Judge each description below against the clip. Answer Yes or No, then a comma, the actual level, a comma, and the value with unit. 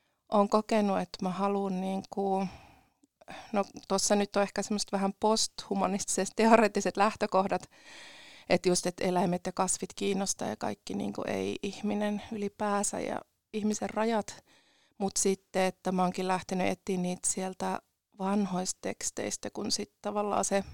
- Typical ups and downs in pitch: No, narrow, 2.1 semitones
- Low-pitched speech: No, high, 200 Hz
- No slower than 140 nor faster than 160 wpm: No, average, 130 wpm